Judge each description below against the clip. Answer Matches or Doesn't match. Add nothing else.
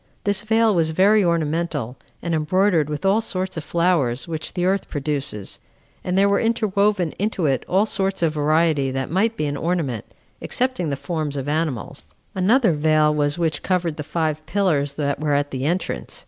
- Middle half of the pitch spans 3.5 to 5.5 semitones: Matches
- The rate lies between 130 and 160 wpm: Doesn't match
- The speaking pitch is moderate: Matches